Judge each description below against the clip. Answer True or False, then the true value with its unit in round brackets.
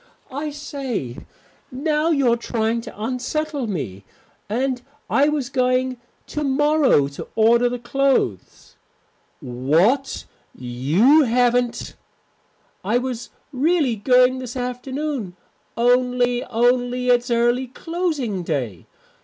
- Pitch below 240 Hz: False (250 Hz)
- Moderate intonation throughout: True (3.2 semitones)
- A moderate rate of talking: False (105 wpm)